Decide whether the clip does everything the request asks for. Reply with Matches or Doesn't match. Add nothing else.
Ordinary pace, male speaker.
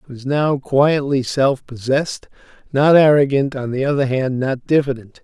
Matches